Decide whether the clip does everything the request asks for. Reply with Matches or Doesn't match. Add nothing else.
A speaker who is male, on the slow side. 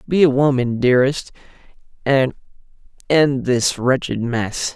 Matches